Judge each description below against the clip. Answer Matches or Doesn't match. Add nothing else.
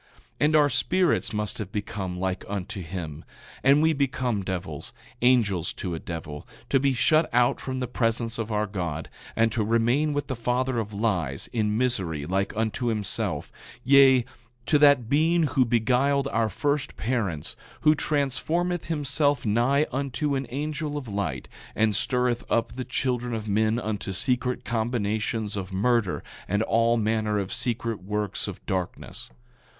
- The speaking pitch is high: Doesn't match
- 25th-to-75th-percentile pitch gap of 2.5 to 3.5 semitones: Doesn't match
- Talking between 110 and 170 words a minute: Matches